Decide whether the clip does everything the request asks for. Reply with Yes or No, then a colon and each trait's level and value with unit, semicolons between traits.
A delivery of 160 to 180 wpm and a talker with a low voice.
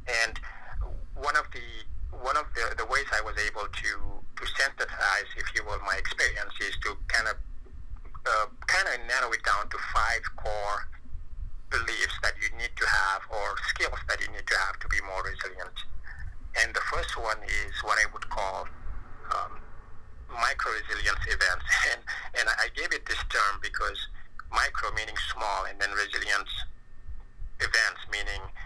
Yes: average, 165 wpm; low, 105 Hz